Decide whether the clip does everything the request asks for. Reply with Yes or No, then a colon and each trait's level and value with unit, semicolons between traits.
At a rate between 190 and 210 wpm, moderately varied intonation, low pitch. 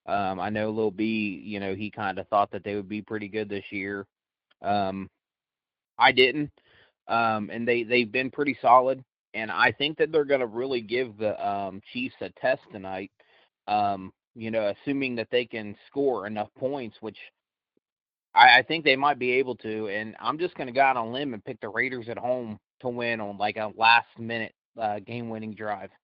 Yes: average, 200 wpm; average, 3.5 semitones; low, 110 Hz